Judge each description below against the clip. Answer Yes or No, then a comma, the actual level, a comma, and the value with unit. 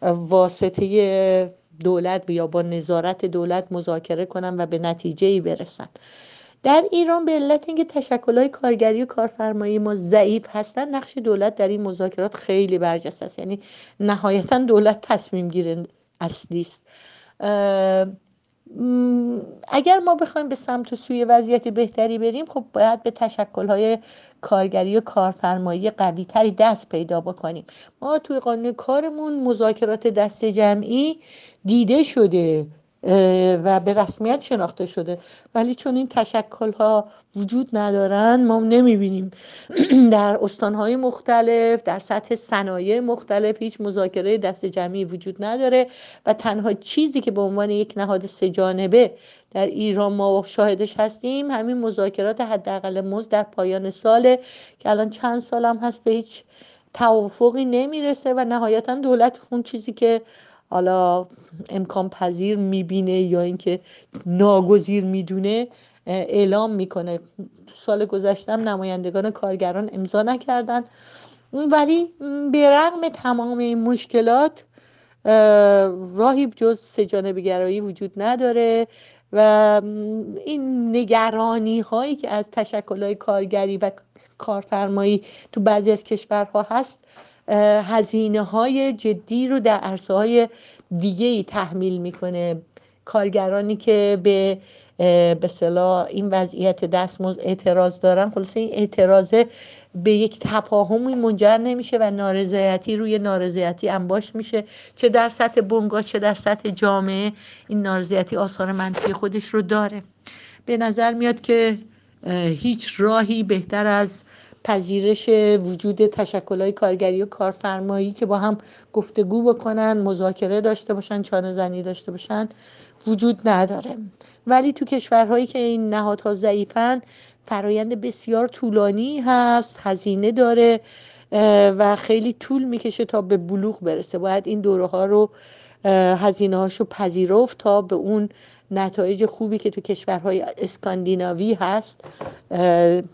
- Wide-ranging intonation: No, average, 3.3 semitones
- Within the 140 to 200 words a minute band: No, average, 125 wpm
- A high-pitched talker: Yes, high, 210 Hz